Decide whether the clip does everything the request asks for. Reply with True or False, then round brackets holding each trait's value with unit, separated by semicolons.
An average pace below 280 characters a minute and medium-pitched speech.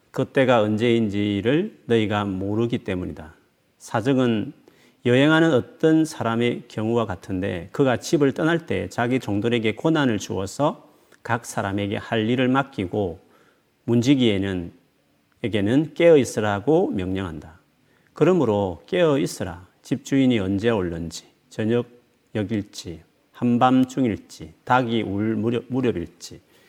False (270 characters per minute; 115 Hz)